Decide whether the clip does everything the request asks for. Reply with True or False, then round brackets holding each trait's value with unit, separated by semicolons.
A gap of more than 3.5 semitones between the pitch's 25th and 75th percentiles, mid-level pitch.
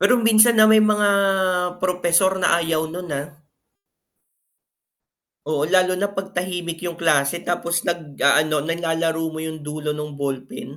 False (2.9 semitones; 170 Hz)